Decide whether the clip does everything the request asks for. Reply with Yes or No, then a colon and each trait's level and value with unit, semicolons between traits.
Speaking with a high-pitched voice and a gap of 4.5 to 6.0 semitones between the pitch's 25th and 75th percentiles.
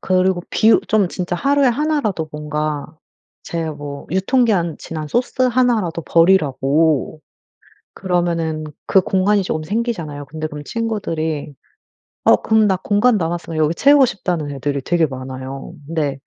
No: medium, 170 Hz; wide, 5.5 semitones